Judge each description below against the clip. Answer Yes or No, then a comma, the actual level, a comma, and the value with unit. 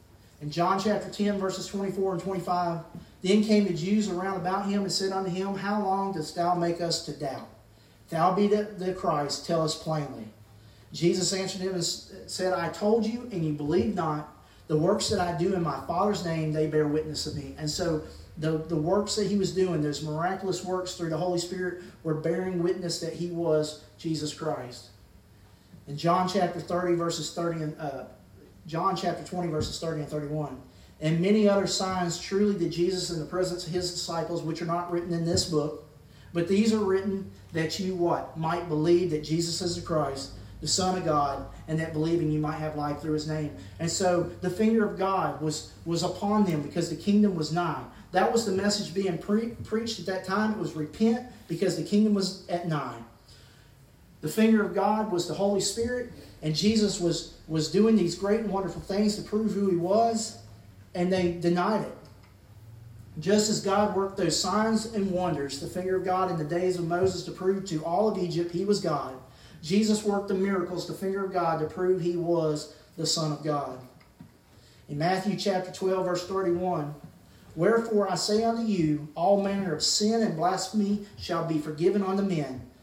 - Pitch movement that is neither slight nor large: Yes, average, 3.8 semitones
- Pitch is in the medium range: Yes, medium, 175 Hz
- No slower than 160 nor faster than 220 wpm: Yes, average, 200 wpm